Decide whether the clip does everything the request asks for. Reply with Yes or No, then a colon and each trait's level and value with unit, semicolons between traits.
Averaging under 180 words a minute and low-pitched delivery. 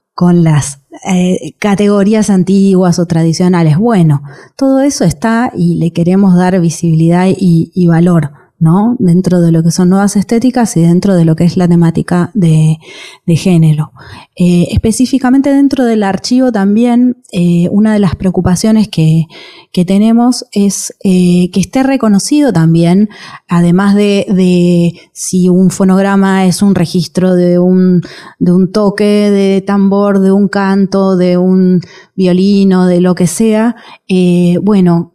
No: average, 145 wpm; medium, 185 Hz